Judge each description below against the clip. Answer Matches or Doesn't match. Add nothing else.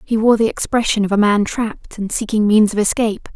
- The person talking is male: Doesn't match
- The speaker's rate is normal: Doesn't match